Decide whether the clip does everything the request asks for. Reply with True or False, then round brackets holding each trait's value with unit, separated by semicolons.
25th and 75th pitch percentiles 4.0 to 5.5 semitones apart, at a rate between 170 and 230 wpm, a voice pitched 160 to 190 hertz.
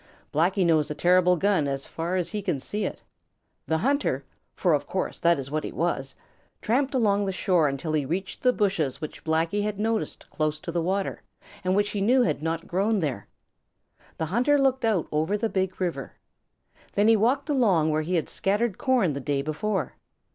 True (5.2 semitones; 200 wpm; 185 Hz)